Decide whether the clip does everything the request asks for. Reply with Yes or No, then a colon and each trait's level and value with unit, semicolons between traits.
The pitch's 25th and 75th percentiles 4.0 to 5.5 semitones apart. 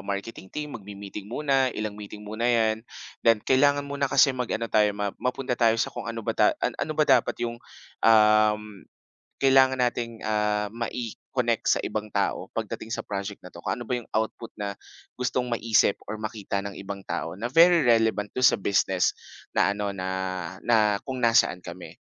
No: average, 3.2 semitones